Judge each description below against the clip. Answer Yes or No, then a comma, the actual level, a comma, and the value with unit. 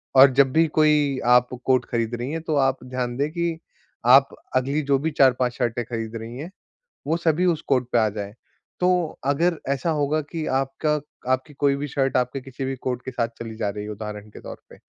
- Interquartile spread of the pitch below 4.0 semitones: Yes, average, 3.4 semitones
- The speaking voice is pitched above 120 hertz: Yes, low, 135 Hz